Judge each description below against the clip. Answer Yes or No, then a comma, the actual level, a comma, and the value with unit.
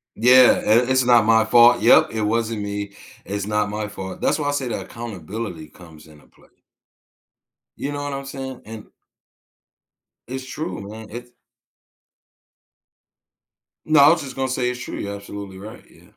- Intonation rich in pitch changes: No, average, 4.1 semitones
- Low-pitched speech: Yes, low, 115 Hz